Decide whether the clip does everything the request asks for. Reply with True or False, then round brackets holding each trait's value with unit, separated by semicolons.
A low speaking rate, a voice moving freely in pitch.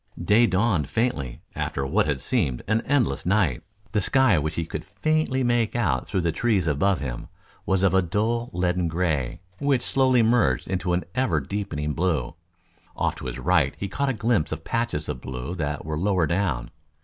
False (185 wpm; 7.1 semitones)